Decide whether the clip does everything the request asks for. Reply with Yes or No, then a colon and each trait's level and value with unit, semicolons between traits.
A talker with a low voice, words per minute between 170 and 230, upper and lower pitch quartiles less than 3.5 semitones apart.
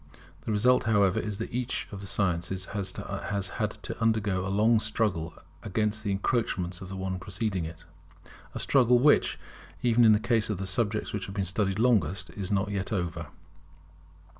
Yes: low, 100 Hz; average, 175 wpm; average, 2.8 semitones